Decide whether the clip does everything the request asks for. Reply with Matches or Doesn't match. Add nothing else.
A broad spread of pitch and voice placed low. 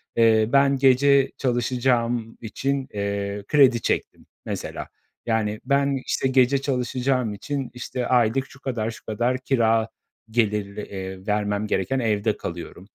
Doesn't match